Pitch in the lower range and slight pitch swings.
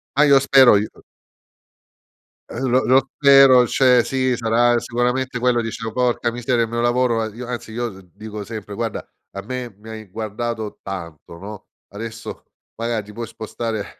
Yes: low, 115 Hz; narrow, 2.3 semitones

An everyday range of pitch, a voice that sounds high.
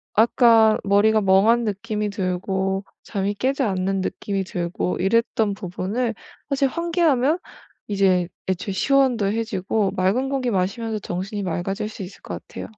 Yes: average, 3.4 semitones; high, 205 Hz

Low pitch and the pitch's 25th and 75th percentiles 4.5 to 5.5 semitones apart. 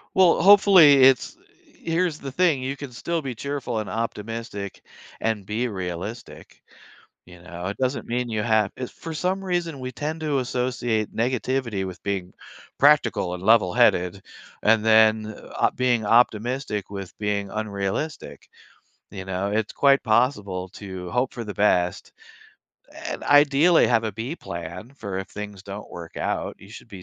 Yes: low, 115 Hz; average, 5.2 semitones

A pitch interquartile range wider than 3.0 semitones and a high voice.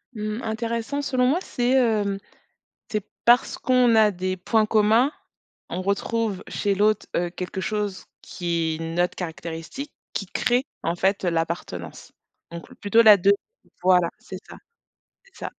Yes: average, 4.4 semitones; high, 205 Hz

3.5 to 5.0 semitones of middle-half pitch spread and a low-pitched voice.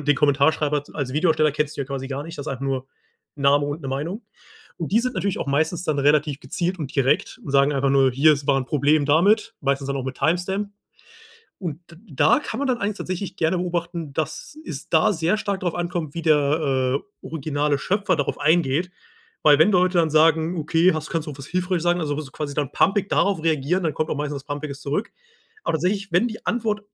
No: average, 3.9 semitones; medium, 155 Hz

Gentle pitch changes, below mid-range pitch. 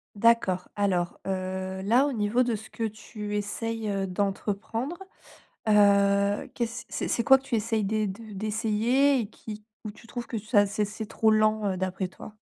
No: narrow, 2.3 semitones; high, 215 Hz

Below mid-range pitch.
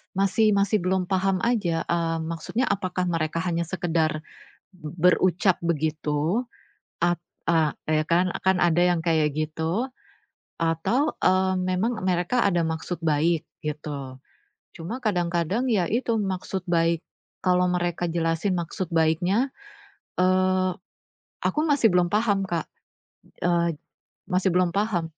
No: medium, 175 Hz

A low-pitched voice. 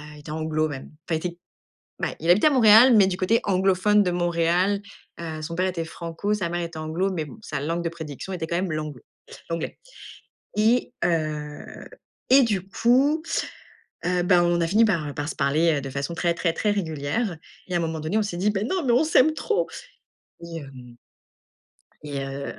No: medium, 175 Hz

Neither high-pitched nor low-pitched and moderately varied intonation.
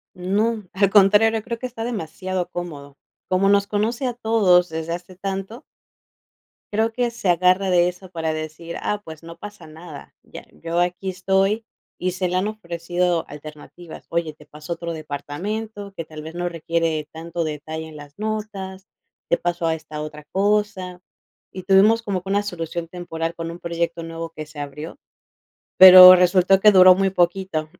Yes: medium, 180 Hz; average, 3.2 semitones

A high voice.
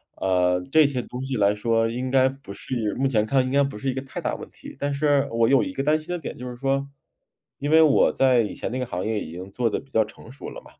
No: low, 130 Hz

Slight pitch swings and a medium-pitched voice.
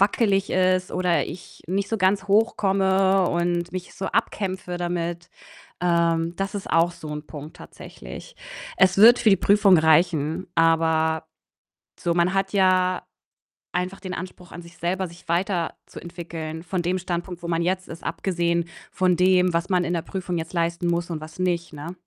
Yes: narrow, 1.9 semitones; medium, 175 Hz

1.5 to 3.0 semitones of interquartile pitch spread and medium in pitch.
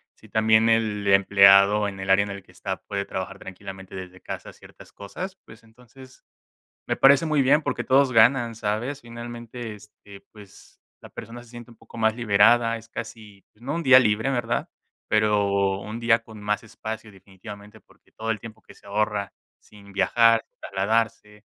No: average, 2.7 semitones; low, 110 Hz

